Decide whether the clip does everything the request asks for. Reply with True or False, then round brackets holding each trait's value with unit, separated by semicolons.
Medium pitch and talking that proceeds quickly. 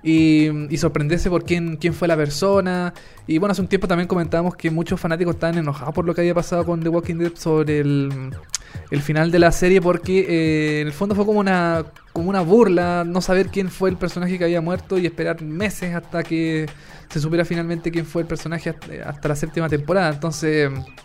True (170 Hz; 215 wpm)